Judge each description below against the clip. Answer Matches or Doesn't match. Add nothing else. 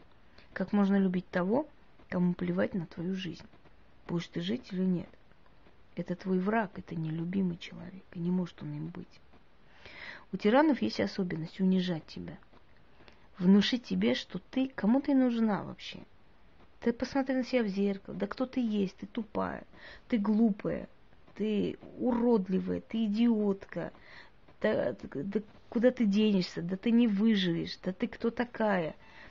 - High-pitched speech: Matches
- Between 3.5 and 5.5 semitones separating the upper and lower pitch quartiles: Matches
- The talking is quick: Doesn't match